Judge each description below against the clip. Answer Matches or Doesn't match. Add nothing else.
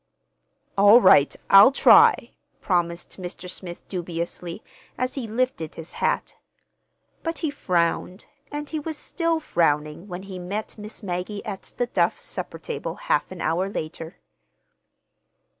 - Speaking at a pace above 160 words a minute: Doesn't match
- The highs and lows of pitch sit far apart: Matches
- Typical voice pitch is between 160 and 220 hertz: Matches